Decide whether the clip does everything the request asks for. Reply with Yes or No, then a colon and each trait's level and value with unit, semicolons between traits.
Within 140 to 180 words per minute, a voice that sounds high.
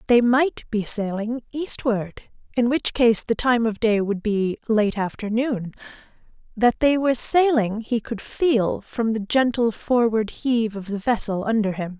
Yes: average, 165 wpm; high, 225 Hz